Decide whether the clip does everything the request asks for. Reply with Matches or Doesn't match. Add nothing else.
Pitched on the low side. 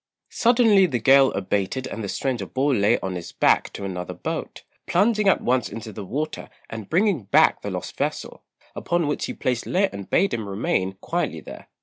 Matches